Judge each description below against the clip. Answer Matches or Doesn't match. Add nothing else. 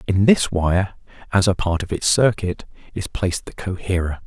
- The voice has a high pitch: Doesn't match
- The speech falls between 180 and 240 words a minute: Doesn't match